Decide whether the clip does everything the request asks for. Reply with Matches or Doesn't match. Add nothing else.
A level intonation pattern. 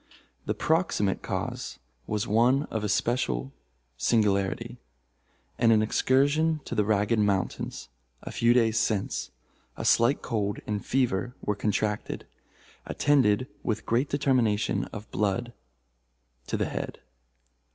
Doesn't match